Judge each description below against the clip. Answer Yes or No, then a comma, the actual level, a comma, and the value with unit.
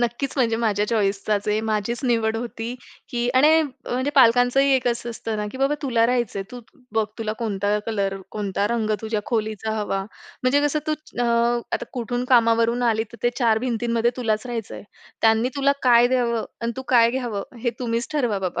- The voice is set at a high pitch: Yes, high, 235 Hz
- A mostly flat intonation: Yes, narrow, 2.2 semitones